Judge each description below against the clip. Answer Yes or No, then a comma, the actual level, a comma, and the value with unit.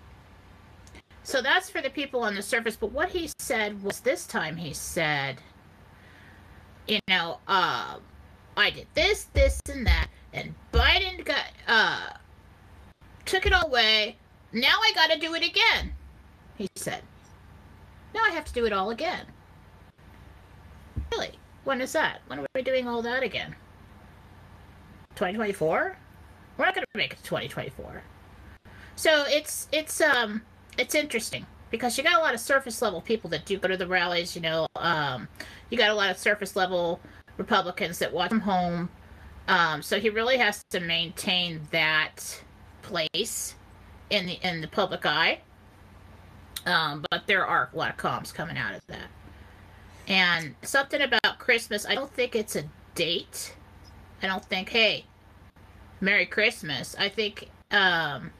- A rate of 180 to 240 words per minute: No, average, 155 wpm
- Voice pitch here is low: No, medium, 185 Hz